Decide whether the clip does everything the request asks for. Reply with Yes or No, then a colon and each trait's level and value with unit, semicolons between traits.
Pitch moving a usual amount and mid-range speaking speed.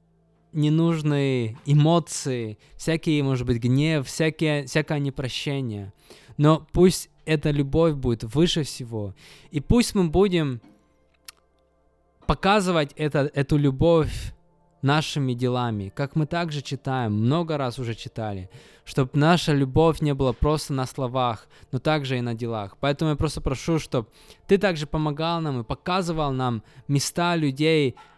Yes: average, 4.2 semitones; average, 130 wpm